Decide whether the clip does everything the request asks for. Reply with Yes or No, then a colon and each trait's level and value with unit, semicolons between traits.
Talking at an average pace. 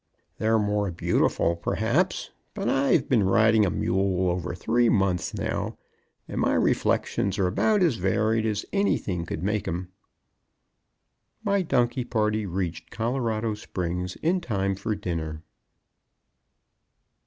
No: slow, 125 wpm